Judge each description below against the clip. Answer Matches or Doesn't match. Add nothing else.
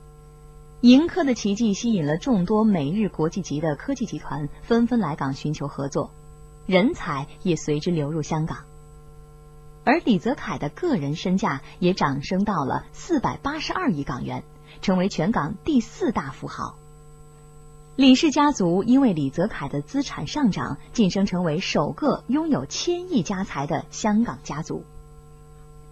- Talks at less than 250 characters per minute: Matches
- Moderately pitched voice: Matches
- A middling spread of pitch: Doesn't match